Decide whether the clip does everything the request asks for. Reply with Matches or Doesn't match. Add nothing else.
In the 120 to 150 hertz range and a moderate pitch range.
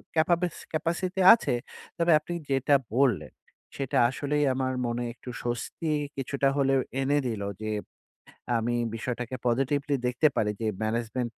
Matches